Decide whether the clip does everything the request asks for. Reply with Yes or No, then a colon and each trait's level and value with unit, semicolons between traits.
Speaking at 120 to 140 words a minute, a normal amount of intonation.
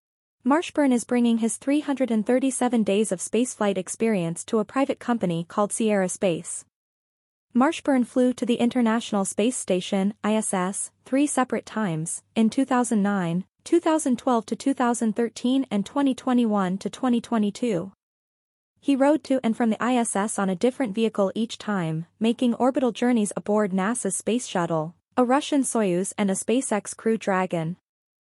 Yes: slow, 135 wpm; average, 4.0 semitones